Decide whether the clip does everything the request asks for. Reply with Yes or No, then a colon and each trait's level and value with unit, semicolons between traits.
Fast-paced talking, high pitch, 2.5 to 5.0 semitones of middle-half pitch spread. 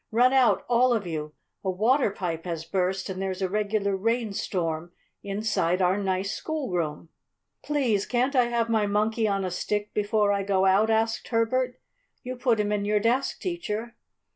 No: average, 175 wpm; high, 210 Hz; average, 3.7 semitones